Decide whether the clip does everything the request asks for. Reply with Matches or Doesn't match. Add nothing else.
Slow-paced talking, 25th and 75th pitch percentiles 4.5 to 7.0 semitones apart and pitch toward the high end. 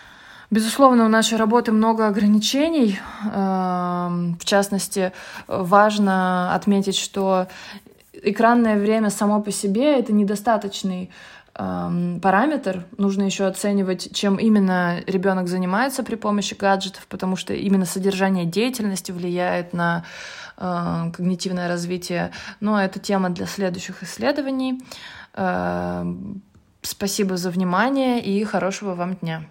Doesn't match